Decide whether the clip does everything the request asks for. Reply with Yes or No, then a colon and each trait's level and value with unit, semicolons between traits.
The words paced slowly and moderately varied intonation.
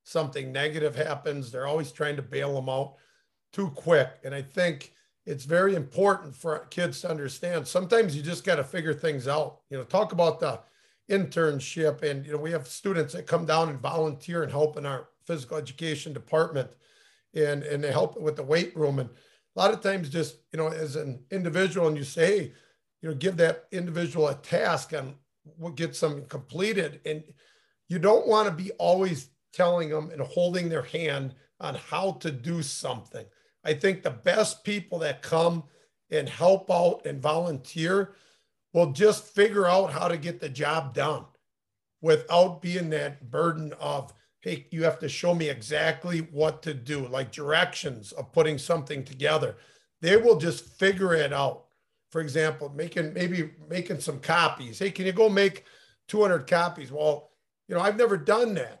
No: average, 180 wpm; average, 3.0 semitones